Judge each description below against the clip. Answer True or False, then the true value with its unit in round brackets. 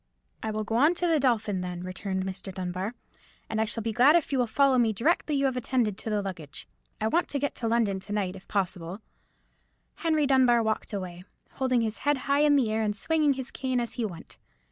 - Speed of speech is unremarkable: False (230 wpm)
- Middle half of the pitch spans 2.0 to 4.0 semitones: False (5.3 semitones)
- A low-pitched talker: False (225 Hz)